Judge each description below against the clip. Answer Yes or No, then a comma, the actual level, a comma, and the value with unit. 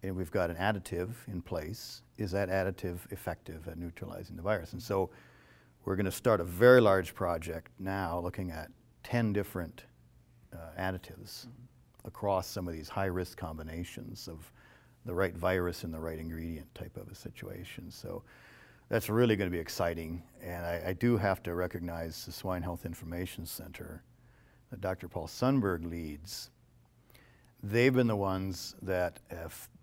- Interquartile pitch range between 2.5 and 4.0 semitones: Yes, average, 3.6 semitones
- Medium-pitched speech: No, very low, 95 Hz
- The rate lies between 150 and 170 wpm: Yes, average, 155 wpm